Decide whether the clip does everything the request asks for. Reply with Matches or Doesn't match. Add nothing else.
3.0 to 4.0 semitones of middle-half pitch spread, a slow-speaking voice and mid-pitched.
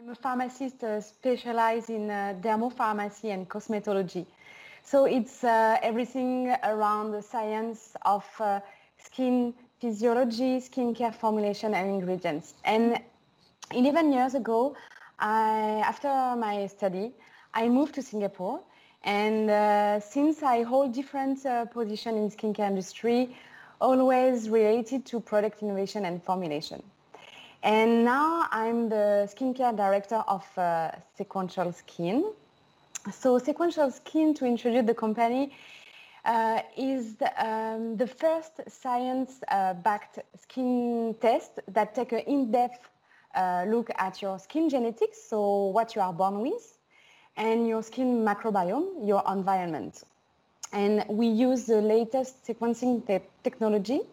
Doesn't match